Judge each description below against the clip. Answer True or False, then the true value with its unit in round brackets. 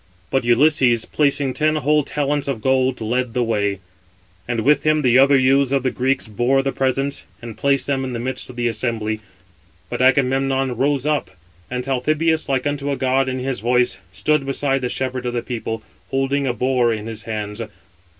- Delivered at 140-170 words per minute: False (195 wpm)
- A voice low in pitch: True (130 Hz)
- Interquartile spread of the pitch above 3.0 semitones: False (2.4 semitones)